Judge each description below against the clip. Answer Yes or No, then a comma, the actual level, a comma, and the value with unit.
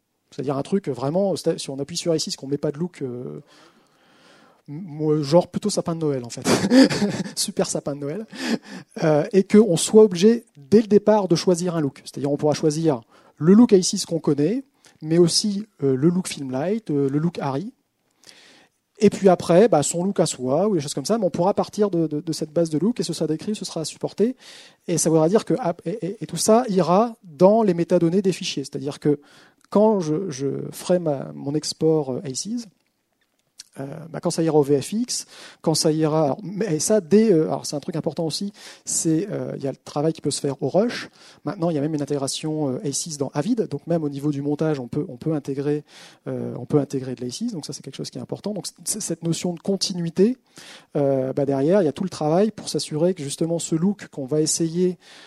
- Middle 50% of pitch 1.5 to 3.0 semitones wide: No, average, 5.0 semitones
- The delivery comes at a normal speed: No, fast, 225 wpm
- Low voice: No, medium, 165 Hz